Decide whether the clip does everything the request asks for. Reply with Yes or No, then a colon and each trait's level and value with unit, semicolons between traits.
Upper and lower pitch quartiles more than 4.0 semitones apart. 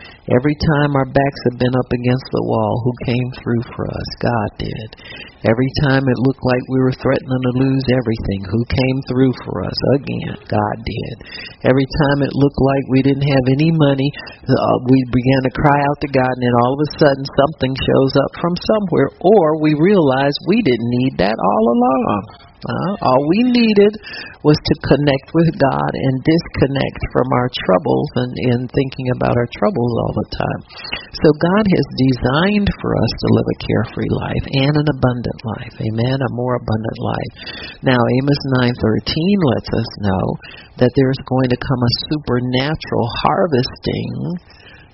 No: narrow, 2.6 semitones